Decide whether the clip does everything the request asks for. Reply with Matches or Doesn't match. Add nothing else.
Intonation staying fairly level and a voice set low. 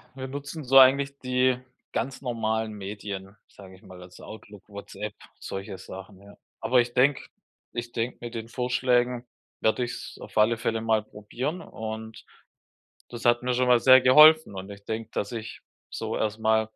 Doesn't match